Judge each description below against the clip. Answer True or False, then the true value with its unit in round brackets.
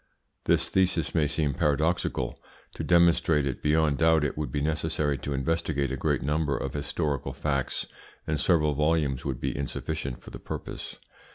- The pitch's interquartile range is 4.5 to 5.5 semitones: False (2.5 semitones)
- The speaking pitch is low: True (75 Hz)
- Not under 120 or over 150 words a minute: False (165 wpm)